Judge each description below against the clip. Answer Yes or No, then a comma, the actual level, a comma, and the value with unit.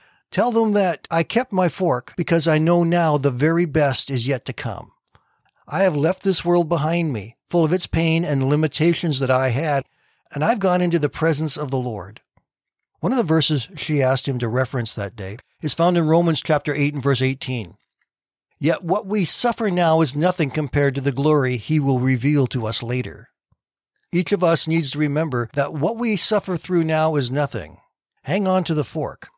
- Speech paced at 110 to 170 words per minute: No, average, 200 wpm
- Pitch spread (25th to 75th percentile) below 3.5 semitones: No, average, 4.2 semitones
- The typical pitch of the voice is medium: Yes, medium, 155 Hz